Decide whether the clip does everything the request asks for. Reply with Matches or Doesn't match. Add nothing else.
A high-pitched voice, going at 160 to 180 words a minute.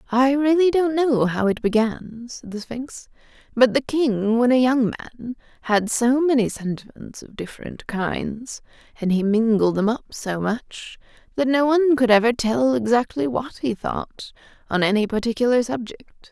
Matches